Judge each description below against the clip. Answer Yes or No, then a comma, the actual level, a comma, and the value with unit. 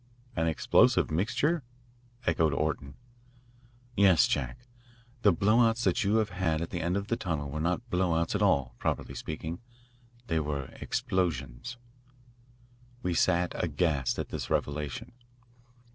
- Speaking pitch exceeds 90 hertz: No, very low, 85 Hz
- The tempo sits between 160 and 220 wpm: No, average, 140 wpm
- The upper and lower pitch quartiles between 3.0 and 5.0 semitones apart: Yes, average, 4.6 semitones